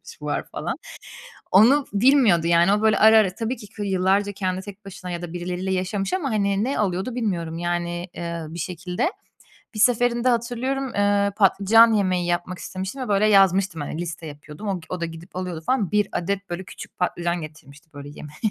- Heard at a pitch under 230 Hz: Yes, high, 190 Hz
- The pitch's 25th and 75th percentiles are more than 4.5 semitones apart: No, average, 3.7 semitones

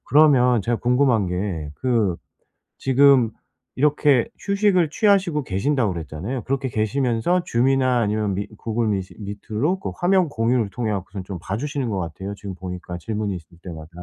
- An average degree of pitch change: No, wide, 6.0 semitones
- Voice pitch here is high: No, low, 115 Hz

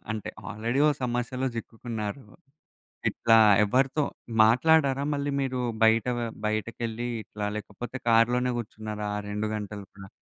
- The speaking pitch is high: No, low, 115 Hz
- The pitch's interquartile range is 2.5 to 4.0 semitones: Yes, average, 2.9 semitones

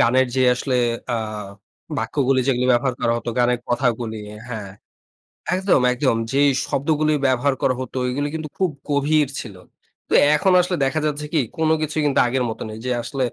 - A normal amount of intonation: Yes, average, 3.5 semitones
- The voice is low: Yes, low, 130 Hz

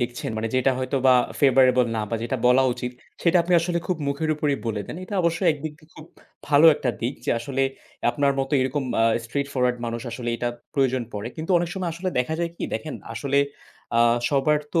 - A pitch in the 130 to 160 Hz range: Yes, low, 135 Hz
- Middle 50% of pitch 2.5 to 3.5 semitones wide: No, average, 4.0 semitones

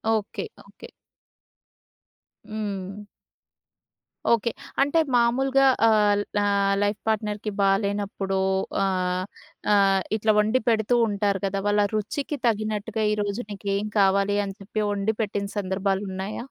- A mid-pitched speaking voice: No, high, 205 Hz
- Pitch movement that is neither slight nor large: No, narrow, 1.6 semitones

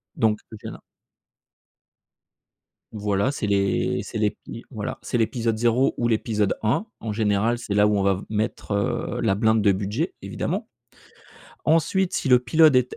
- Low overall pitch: Yes, low, 110 Hz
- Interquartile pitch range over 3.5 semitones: No, average, 2.9 semitones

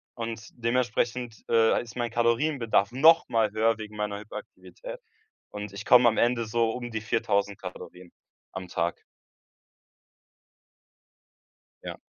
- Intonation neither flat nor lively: No, narrow, 2.3 semitones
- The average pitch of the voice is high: No, low, 115 Hz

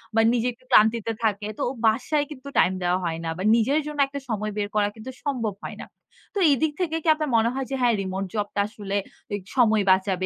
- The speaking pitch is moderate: No, high, 220 Hz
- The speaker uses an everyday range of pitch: Yes, average, 4.5 semitones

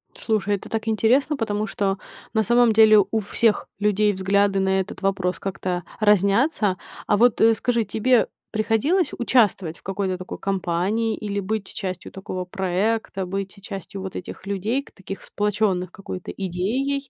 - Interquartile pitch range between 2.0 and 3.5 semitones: Yes, average, 2.7 semitones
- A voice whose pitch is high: Yes, high, 205 Hz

